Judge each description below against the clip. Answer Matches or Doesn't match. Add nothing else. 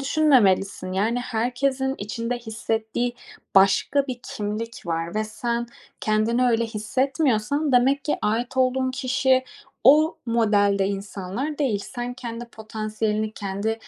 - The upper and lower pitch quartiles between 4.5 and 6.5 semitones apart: Doesn't match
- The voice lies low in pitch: Doesn't match